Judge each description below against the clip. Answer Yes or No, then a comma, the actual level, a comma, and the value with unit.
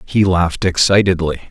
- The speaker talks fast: No, slow, 120 wpm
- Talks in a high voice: No, very low, 90 Hz